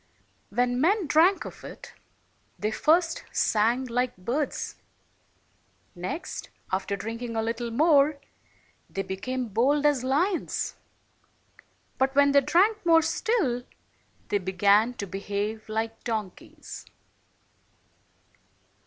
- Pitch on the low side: No, high, 245 Hz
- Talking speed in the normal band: No, slow, 105 wpm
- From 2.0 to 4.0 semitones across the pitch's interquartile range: No, wide, 5.5 semitones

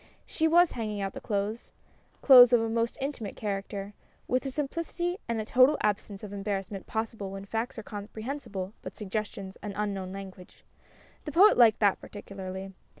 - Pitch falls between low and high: No, high, 210 Hz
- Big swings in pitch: No, average, 3.8 semitones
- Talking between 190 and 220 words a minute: No, average, 165 wpm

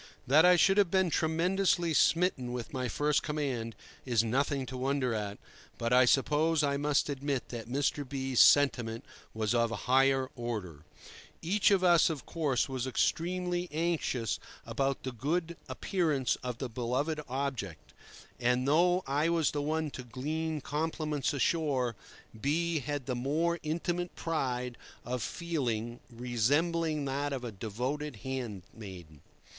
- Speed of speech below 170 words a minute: Yes, average, 145 wpm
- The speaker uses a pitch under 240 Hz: Yes, medium, 140 Hz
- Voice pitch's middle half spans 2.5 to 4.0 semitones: No, average, 4.5 semitones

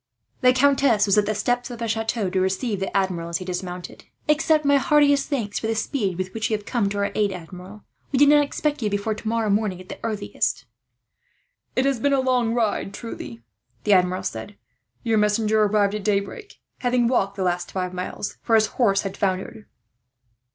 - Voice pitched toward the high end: Yes, high, 215 Hz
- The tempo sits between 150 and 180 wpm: No, average, 200 wpm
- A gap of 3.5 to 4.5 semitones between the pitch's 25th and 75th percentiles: Yes, average, 4.1 semitones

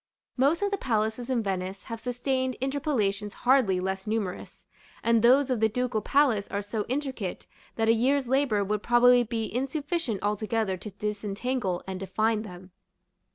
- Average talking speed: Yes, average, 155 wpm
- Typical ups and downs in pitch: Yes, average, 4.1 semitones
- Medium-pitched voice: No, high, 225 Hz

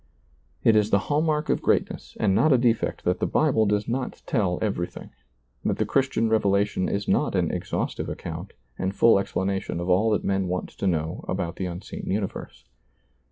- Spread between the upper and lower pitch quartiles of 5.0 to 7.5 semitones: No, average, 3.1 semitones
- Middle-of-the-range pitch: No, low, 100 Hz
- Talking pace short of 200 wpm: Yes, average, 185 wpm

